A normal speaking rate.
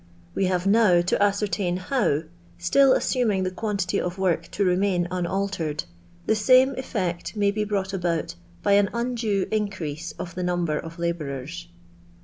Yes: average, 160 wpm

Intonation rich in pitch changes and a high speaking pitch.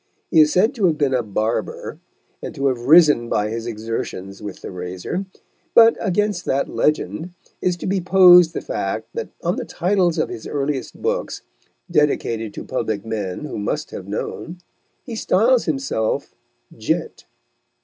No: wide, 8.3 semitones; medium, 150 Hz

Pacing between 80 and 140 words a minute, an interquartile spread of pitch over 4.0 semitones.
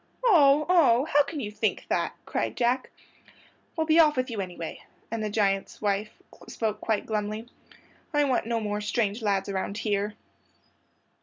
No: average, 160 wpm; average, 5.1 semitones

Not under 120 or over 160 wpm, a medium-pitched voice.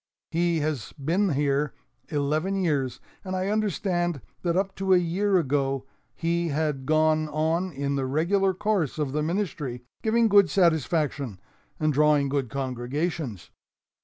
Yes: average, 140 wpm; medium, 155 Hz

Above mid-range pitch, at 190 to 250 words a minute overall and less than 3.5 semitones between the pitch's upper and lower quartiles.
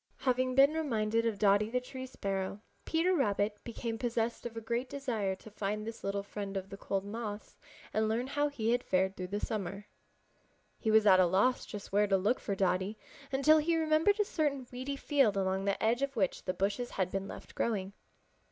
No: high, 220 Hz; fast, 205 wpm; average, 4.5 semitones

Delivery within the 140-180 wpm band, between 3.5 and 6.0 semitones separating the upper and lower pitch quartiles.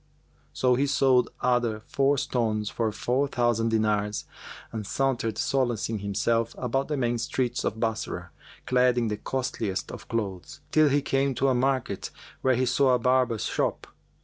No: average, 160 wpm; average, 3.0 semitones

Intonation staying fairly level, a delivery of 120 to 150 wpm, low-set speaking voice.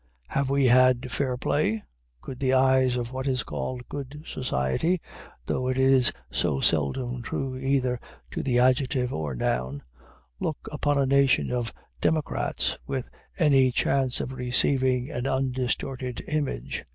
Yes: narrow, 1.6 semitones; average, 140 wpm; low, 130 Hz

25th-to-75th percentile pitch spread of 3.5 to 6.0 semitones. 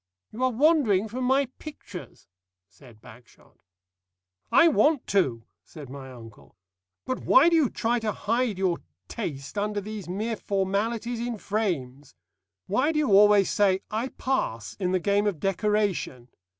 Yes: average, 5.1 semitones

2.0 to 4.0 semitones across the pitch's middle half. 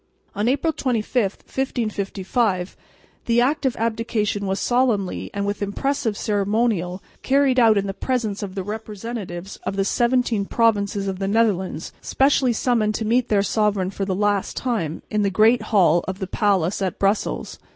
Yes: average, 3.3 semitones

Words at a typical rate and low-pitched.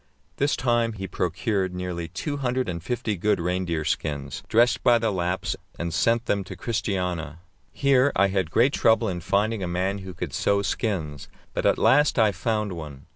Yes: average, 180 wpm; very low, 95 Hz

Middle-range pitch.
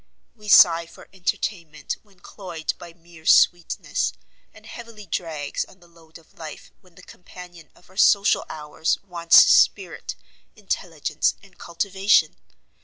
Yes: medium, 175 Hz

